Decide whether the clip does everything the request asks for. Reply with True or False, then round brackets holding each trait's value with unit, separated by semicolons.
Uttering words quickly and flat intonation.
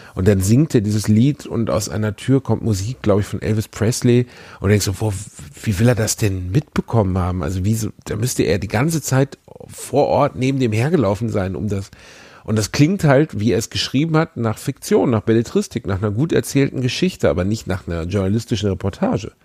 False (210 wpm; 4.3 semitones)